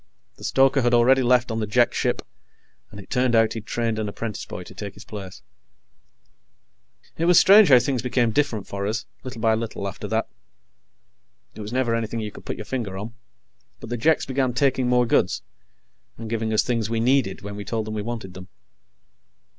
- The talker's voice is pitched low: Yes, low, 115 Hz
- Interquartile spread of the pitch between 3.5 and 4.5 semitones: No, average, 2.7 semitones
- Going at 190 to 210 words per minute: Yes, average, 200 wpm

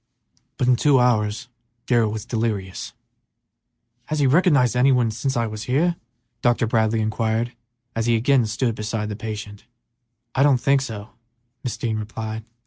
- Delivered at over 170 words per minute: No, average, 155 wpm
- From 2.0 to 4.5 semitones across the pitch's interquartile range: Yes, average, 2.7 semitones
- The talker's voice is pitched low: Yes, low, 115 Hz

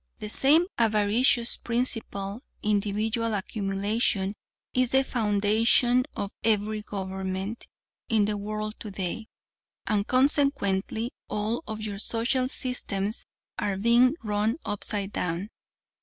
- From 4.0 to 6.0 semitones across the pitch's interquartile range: No, average, 2.7 semitones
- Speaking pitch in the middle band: No, high, 215 Hz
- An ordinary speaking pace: No, slow, 105 wpm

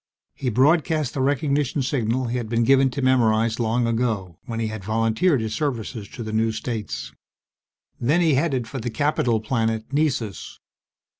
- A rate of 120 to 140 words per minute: No, average, 165 wpm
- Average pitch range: Yes, average, 3.6 semitones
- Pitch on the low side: Yes, low, 120 Hz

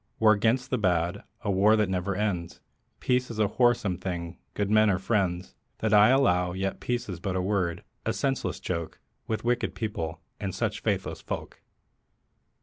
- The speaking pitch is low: Yes, low, 100 Hz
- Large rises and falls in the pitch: No, average, 3.5 semitones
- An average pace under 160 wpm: No, average, 175 wpm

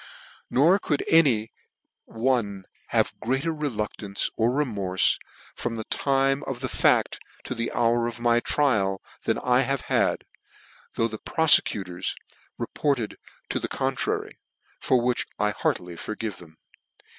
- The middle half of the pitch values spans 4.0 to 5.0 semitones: Yes, average, 4.4 semitones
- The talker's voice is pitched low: Yes, low, 120 Hz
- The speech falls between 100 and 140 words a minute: Yes, slow, 135 wpm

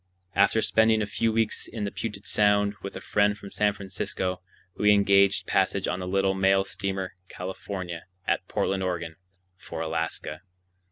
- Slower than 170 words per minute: Yes, average, 160 wpm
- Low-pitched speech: Yes, low, 100 Hz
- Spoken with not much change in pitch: Yes, narrow, 1.8 semitones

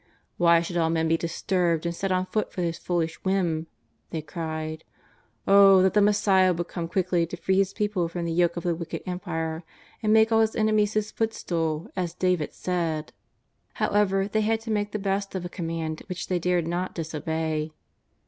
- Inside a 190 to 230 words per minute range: Yes, fast, 205 wpm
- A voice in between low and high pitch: Yes, medium, 180 Hz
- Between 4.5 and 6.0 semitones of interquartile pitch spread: No, average, 3.0 semitones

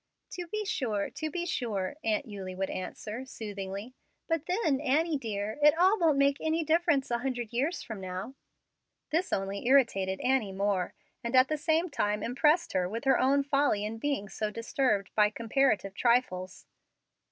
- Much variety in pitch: Yes, wide, 6.5 semitones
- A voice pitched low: No, very high, 250 Hz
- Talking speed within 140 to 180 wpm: Yes, average, 170 wpm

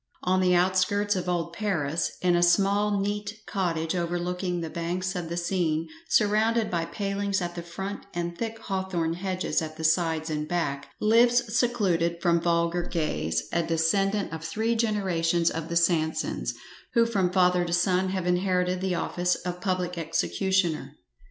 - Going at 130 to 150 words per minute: No, average, 160 wpm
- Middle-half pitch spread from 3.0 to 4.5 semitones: No, narrow, 2.6 semitones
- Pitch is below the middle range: No, medium, 180 Hz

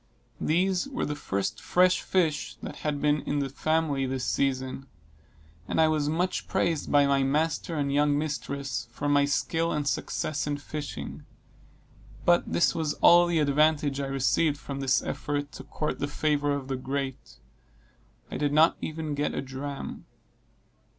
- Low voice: No, medium, 145 Hz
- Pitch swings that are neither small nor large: No, narrow, 2.1 semitones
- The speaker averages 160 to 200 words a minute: Yes, average, 165 wpm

